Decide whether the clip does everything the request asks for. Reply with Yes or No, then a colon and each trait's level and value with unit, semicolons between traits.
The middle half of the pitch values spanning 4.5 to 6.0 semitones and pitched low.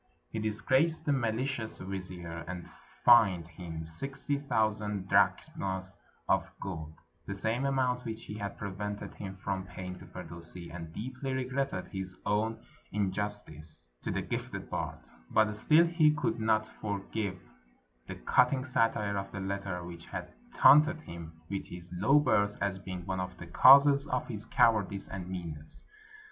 Yes: average, 4.9 semitones; low, 100 Hz